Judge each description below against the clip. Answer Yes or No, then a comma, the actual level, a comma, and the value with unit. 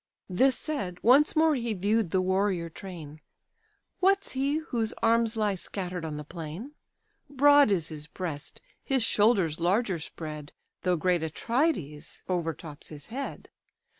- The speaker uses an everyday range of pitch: No, wide, 6.9 semitones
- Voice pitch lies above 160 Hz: Yes, high, 190 Hz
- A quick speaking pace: No, slow, 135 wpm